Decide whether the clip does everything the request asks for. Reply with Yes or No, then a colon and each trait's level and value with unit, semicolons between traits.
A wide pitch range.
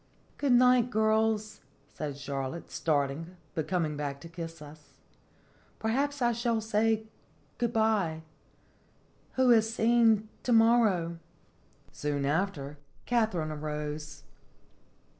Yes: wide, 6.9 semitones